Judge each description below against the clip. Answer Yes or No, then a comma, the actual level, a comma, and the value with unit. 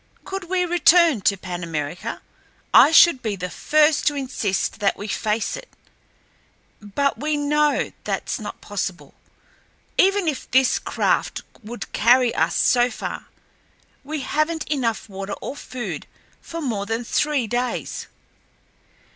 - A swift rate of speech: No, slow, 135 wpm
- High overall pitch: Yes, very high, 255 Hz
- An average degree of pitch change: No, wide, 6.3 semitones